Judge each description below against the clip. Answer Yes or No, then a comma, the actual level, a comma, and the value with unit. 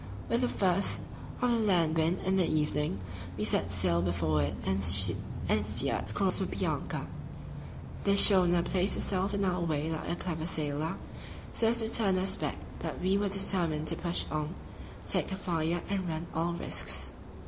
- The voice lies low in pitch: No, medium, 175 Hz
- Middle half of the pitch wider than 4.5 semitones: No, average, 3.8 semitones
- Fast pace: No, average, 175 wpm